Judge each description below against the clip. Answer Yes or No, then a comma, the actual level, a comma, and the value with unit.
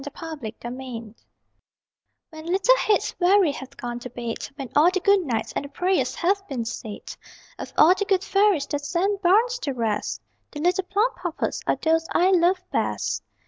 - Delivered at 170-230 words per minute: Yes, average, 180 wpm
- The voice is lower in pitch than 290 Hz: No, very high, 335 Hz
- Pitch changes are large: Yes, wide, 6.4 semitones